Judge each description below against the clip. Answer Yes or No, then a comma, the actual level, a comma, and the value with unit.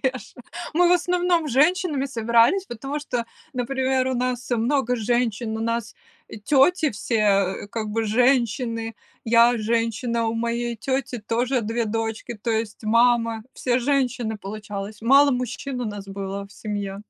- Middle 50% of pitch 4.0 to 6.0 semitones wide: No, average, 2.9 semitones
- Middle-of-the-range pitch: No, high, 235 Hz